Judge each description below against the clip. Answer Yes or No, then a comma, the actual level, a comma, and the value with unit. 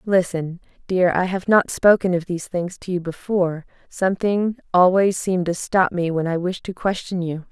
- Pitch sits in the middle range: Yes, medium, 180 Hz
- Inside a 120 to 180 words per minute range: No, average, 190 wpm